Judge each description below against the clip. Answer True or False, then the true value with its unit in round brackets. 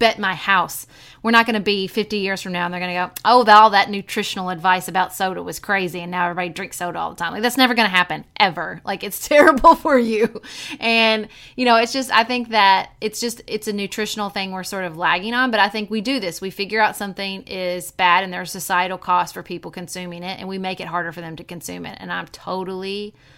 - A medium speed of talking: False (250 wpm)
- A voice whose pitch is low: False (195 Hz)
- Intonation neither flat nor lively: True (3.4 semitones)